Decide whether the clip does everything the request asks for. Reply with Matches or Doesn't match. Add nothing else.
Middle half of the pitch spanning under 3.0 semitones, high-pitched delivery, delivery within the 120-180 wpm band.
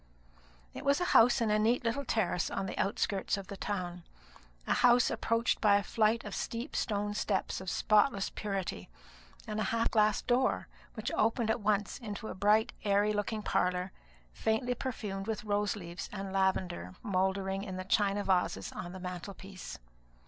Matches